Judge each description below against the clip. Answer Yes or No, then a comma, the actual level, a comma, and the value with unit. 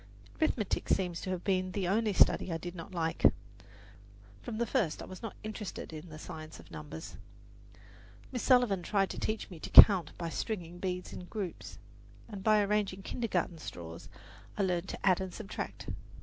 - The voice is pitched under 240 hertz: Yes, medium, 185 Hz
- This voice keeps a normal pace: Yes, average, 180 wpm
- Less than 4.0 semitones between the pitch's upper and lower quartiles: Yes, average, 3.6 semitones